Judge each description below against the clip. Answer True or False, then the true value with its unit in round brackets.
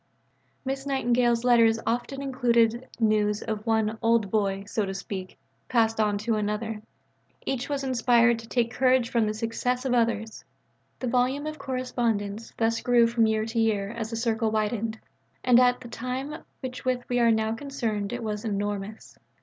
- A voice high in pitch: True (230 Hz)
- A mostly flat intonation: True (2.3 semitones)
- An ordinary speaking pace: True (170 wpm)